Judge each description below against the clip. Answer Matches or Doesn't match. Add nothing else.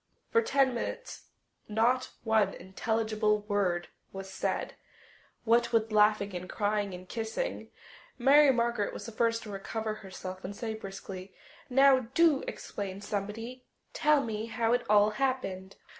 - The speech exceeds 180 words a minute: Doesn't match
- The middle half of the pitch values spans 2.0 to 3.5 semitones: Matches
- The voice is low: Doesn't match